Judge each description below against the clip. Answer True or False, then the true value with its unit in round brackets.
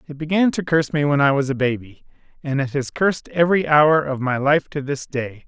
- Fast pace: True (240 wpm)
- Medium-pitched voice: True (145 Hz)